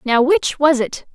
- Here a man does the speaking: No, female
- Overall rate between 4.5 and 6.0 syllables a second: No, 4.0 syllables/s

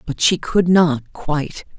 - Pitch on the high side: No, medium, 160 Hz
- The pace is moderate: Yes, average, 170 wpm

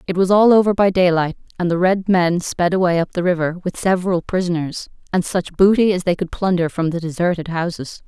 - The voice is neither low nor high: Yes, medium, 180 Hz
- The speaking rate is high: Yes, fast, 215 wpm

